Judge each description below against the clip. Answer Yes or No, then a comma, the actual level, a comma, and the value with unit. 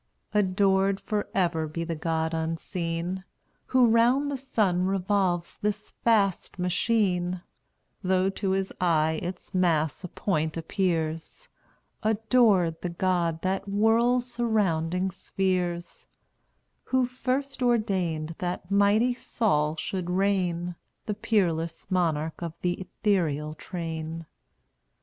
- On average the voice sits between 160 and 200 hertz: Yes, medium, 185 Hz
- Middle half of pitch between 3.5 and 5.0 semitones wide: Yes, average, 3.8 semitones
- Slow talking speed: Yes, slow, 110 wpm